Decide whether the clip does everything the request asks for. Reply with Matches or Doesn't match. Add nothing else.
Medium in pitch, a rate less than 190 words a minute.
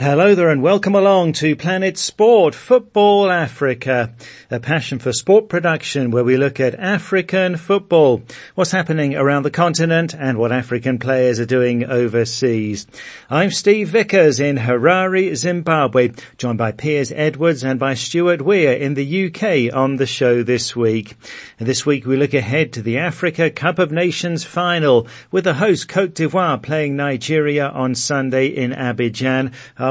Matches